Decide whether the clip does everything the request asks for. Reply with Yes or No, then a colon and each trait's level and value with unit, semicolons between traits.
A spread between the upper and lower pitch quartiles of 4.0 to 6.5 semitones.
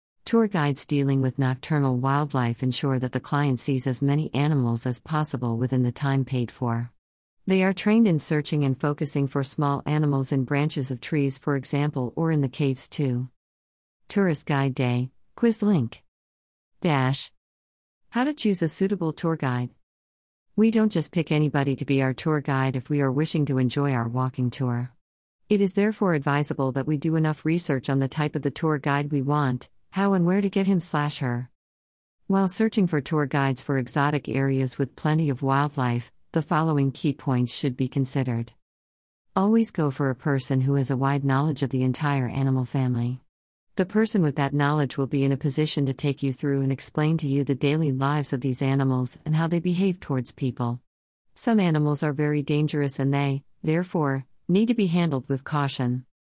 No: average, 3.0 semitones